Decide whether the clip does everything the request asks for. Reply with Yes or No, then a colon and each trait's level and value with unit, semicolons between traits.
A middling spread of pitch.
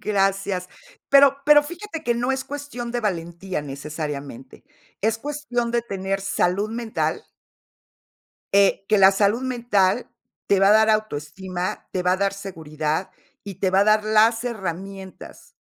Yes: average, 4.3 semitones